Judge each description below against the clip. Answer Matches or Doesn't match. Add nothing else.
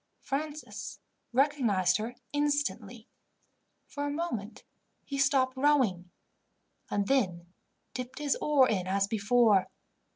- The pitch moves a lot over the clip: Matches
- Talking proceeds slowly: Matches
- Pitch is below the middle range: Doesn't match